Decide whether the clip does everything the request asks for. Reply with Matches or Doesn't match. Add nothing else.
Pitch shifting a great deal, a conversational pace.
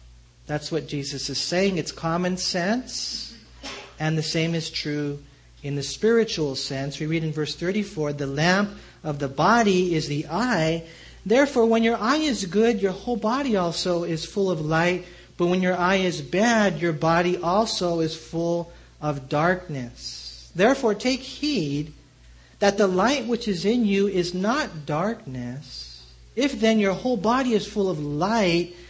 Matches